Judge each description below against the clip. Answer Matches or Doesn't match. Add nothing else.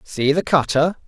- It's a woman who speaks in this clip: Doesn't match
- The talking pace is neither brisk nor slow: Matches